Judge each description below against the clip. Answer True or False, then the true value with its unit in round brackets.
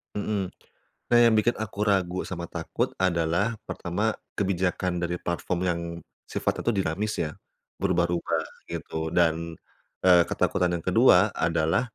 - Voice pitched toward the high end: False (90 Hz)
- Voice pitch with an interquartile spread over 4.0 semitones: False (2.7 semitones)